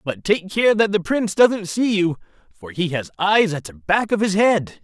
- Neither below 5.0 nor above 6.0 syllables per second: No, 4.6 syllables/s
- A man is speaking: Yes, male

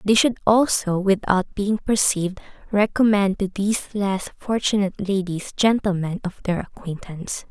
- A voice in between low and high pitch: No, high, 200 Hz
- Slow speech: Yes, slow, 130 wpm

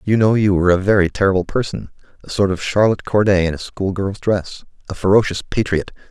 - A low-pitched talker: Yes, low, 100 Hz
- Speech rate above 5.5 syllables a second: Yes, 6.1 syllables/s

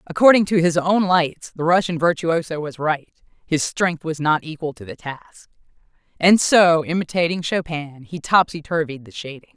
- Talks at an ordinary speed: Yes, average, 170 wpm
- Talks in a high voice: No, medium, 165 Hz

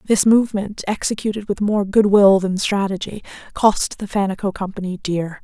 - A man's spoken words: No, female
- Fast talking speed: No, average, 155 wpm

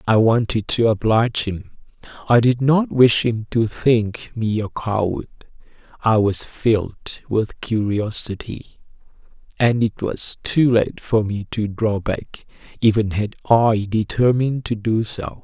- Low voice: Yes, low, 110 Hz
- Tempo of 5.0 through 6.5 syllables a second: No, 4.0 syllables/s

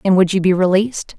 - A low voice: No, high, 190 Hz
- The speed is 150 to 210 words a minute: No, fast, 255 wpm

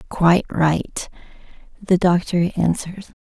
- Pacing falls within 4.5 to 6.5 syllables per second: No, 3.7 syllables/s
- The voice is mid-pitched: Yes, medium, 175 Hz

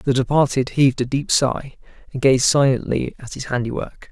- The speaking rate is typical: Yes, average, 175 wpm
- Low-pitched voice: Yes, low, 130 Hz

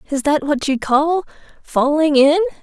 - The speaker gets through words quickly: No, average, 160 wpm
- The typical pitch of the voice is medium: No, very high, 300 Hz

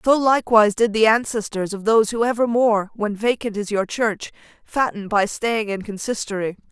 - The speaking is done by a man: No, female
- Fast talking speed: No, average, 170 wpm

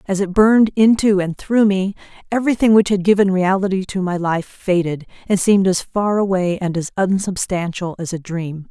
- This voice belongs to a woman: Yes, female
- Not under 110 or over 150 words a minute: No, average, 185 wpm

